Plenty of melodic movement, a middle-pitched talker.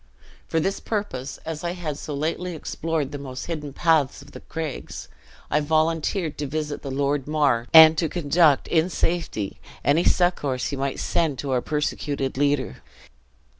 No: narrow, 2.6 semitones; medium, 150 Hz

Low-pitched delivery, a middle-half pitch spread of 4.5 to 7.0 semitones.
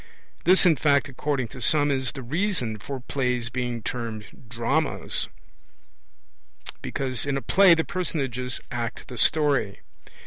No: low, 130 Hz; average, 3.7 semitones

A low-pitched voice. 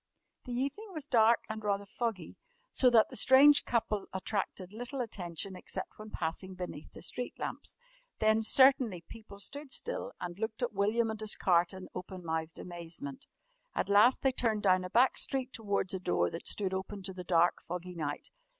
No: high, 205 Hz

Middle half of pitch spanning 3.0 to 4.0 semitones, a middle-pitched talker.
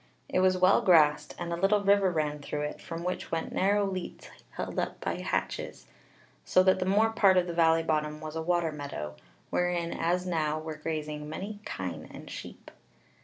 Yes: average, 3.3 semitones; medium, 170 Hz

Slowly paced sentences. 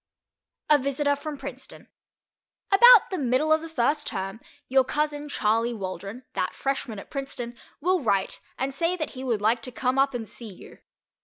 No: average, 175 wpm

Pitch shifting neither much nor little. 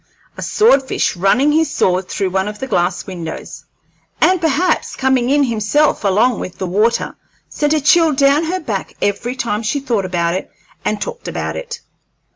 No: wide, 7.3 semitones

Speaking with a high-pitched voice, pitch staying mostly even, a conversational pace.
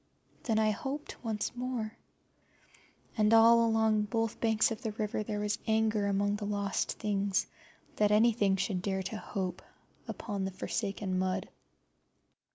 Yes: high, 210 Hz; narrow, 1.8 semitones; average, 145 wpm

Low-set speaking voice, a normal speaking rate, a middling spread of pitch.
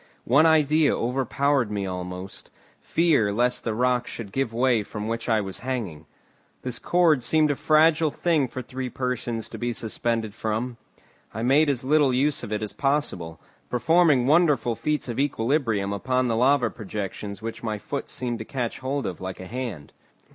Yes: low, 125 Hz; average, 175 wpm; average, 4.4 semitones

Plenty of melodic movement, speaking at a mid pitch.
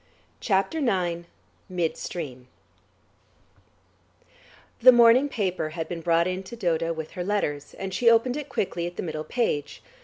Yes: wide, 5.7 semitones; medium, 180 Hz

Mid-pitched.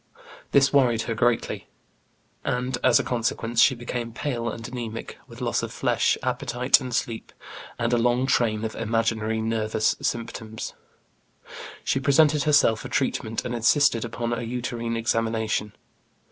No: low, 115 Hz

